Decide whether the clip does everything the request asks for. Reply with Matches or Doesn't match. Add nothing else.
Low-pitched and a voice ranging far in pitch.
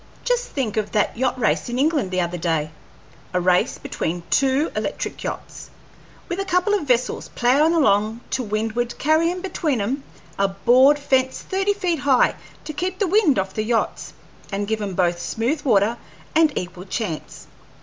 Doesn't match